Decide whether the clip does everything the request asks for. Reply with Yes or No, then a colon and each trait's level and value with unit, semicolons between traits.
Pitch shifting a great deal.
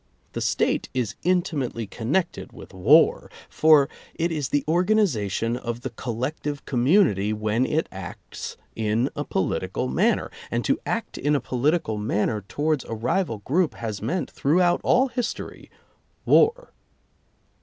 Yes: wide, 6.9 semitones